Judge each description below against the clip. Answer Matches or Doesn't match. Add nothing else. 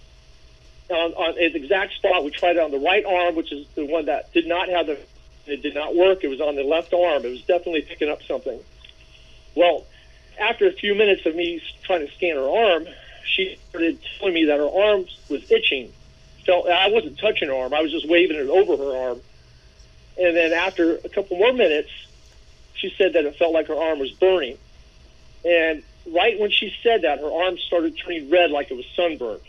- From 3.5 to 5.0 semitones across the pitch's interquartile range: Matches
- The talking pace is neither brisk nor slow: Doesn't match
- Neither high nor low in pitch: Matches